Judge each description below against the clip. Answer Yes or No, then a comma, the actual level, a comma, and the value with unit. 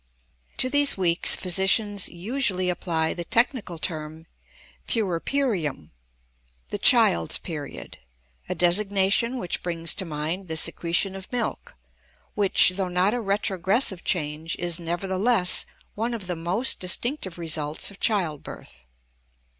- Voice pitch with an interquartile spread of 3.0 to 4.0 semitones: Yes, average, 3.6 semitones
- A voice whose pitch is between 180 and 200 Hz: Yes, medium, 185 Hz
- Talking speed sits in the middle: No, slow, 120 wpm